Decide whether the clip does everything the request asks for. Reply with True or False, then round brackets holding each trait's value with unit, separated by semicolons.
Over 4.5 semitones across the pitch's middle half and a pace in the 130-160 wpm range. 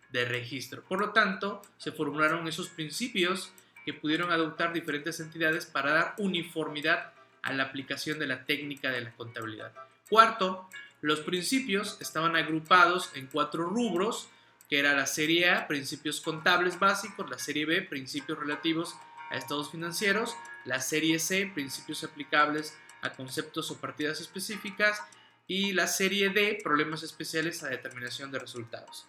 False (3.8 semitones; 145 wpm)